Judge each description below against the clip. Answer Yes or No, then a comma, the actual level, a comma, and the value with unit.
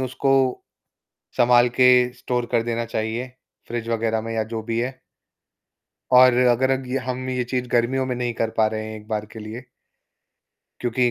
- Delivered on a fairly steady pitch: Yes, narrow, 1.9 semitones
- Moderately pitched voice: No, low, 120 Hz